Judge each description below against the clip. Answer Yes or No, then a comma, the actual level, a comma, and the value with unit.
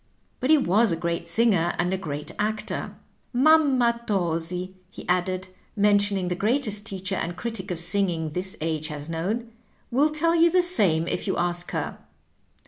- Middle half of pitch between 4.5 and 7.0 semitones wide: Yes, average, 5.3 semitones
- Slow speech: No, average, 170 wpm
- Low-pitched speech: No, high, 190 Hz